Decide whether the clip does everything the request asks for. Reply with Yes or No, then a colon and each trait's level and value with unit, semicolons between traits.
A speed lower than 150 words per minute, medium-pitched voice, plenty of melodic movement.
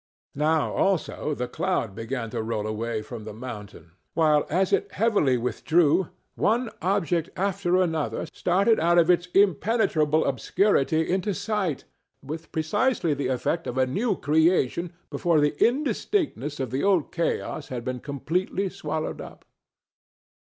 Yes: average, 140 wpm; medium, 160 Hz; wide, 6.3 semitones